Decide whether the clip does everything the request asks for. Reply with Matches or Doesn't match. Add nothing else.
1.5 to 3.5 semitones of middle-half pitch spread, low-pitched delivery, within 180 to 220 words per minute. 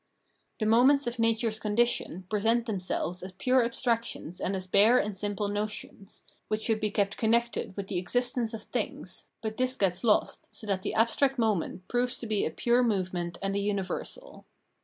Doesn't match